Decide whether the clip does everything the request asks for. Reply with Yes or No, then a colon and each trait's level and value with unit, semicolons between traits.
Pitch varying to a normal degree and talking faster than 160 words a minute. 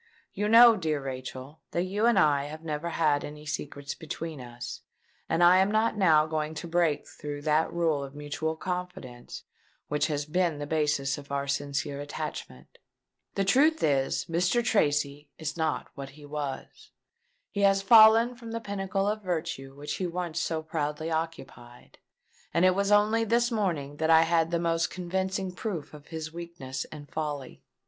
Yes: average, 4.4 semitones; average, 170 wpm